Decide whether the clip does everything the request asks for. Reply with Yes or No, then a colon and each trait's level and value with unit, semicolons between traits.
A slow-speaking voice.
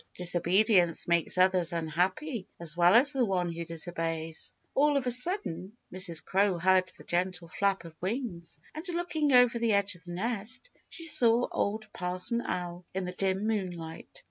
No: average, 170 wpm